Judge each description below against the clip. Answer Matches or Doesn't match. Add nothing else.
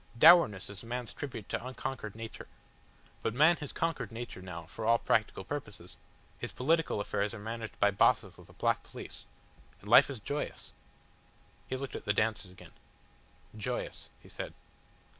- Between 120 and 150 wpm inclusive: Doesn't match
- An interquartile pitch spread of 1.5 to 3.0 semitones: Doesn't match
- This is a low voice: Matches